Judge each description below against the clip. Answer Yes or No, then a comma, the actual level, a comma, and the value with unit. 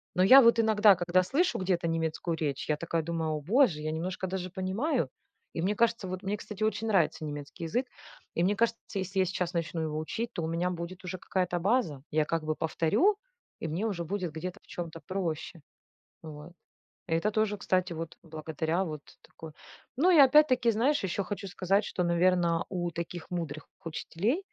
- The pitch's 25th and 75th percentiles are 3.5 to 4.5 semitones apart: Yes, average, 4.0 semitones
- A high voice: No, medium, 180 Hz